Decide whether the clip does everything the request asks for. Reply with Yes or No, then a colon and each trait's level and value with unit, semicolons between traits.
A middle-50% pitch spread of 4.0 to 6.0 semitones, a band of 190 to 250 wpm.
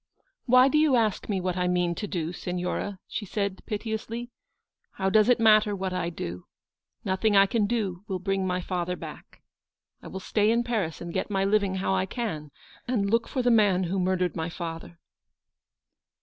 No: average, 3.4 semitones; average, 200 wpm